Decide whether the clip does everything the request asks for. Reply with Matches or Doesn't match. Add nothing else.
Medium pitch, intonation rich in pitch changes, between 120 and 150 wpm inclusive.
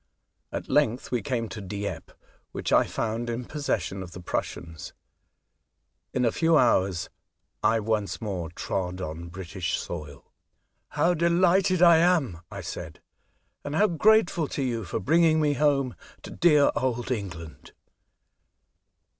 Doesn't match